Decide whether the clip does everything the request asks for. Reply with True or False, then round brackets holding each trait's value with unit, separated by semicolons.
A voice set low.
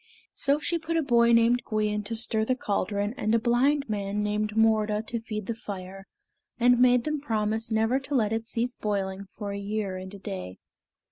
False (220 Hz)